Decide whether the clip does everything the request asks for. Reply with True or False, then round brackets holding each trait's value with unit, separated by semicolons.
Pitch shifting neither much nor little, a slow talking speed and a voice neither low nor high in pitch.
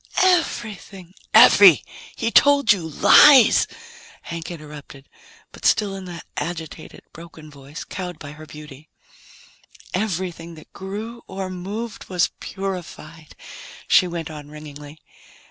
True (4.3 semitones; 125 wpm; 175 Hz)